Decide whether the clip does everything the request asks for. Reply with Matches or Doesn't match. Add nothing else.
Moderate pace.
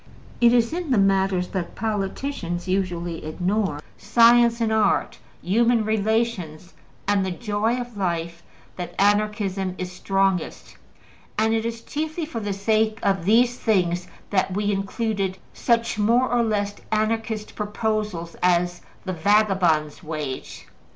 Doesn't match